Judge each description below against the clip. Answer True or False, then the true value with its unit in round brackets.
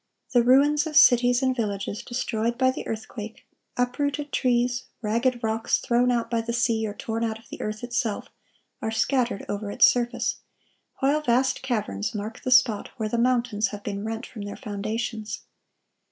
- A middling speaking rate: True (170 wpm)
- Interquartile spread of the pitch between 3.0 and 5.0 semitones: False (2.4 semitones)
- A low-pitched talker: False (235 Hz)